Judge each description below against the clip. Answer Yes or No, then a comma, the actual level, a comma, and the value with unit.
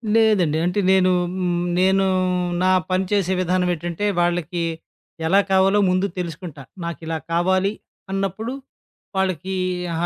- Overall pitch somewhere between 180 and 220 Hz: Yes, medium, 185 Hz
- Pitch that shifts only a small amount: Yes, narrow, 1.8 semitones